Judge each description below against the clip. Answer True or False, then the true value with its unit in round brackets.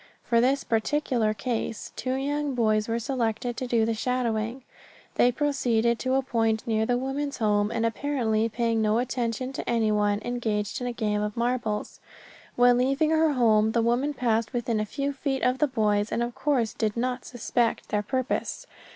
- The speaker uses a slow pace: False (180 wpm)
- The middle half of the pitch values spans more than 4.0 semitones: False (2.7 semitones)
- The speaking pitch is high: True (235 Hz)